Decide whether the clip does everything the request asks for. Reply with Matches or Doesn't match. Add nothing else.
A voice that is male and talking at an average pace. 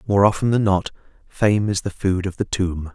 Doesn't match